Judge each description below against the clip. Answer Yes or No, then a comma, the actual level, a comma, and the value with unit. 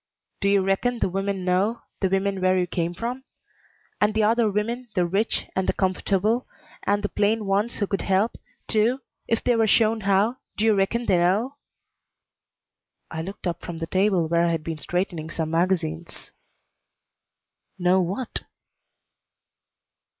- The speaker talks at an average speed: Yes, average, 160 wpm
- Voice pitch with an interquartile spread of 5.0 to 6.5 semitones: No, average, 3.4 semitones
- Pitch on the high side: Yes, high, 195 Hz